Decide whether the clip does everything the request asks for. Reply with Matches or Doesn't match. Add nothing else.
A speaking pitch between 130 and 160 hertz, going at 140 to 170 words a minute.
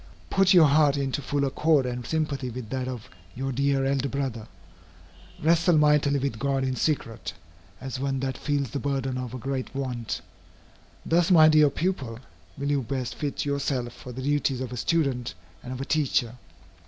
Doesn't match